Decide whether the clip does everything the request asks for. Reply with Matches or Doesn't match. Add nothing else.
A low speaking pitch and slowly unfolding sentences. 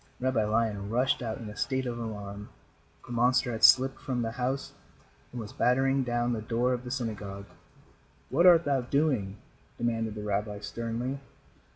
Doesn't match